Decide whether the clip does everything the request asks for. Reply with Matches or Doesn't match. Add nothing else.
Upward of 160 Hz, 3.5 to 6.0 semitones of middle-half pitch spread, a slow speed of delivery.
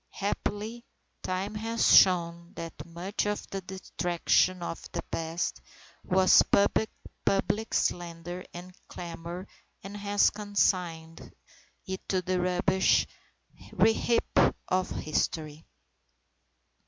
Doesn't match